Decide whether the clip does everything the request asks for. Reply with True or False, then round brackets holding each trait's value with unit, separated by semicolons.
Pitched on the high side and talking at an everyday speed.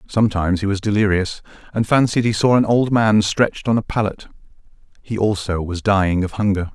False (105 Hz; 185 wpm)